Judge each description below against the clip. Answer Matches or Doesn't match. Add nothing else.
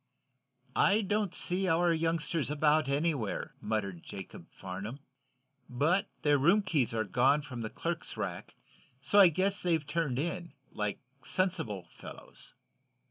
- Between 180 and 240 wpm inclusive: Doesn't match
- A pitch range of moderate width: Doesn't match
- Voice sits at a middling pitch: Matches